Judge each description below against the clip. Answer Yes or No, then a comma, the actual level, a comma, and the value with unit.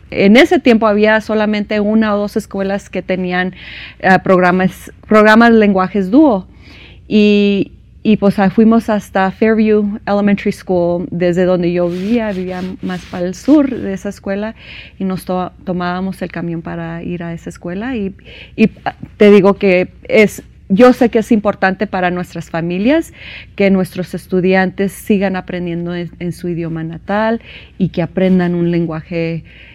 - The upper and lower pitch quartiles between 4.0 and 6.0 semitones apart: No, average, 3.1 semitones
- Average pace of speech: Yes, average, 155 wpm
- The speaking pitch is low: No, high, 190 Hz